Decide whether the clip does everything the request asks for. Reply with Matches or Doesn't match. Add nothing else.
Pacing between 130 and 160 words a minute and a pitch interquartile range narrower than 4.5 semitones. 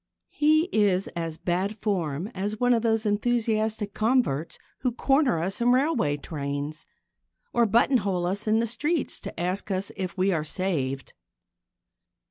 Doesn't match